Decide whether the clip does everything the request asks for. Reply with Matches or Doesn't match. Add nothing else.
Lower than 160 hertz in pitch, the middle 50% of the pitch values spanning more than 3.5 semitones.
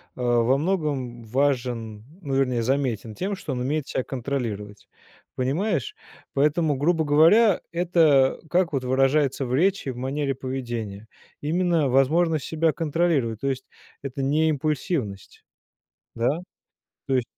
Matches